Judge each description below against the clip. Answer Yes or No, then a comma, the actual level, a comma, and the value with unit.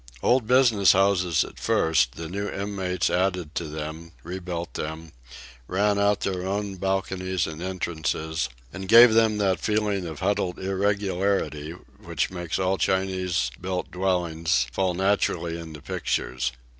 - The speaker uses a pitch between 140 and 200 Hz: No, very low, 95 Hz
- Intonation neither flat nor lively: Yes, average, 3.0 semitones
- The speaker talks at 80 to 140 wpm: Yes, slow, 135 wpm